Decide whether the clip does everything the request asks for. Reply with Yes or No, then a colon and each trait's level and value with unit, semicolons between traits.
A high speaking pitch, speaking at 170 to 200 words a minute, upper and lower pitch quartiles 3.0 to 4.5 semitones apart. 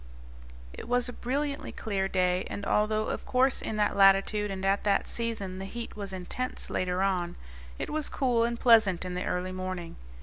Yes: high, 200 Hz; average, 190 wpm; average, 4.0 semitones